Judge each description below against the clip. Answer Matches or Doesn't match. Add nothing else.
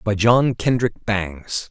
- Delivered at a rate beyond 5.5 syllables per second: Doesn't match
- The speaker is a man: Matches